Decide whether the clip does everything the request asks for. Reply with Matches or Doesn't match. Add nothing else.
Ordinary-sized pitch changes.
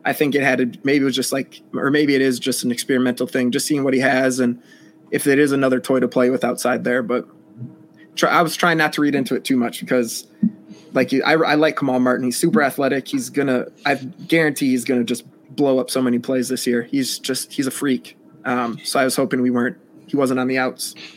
Doesn't match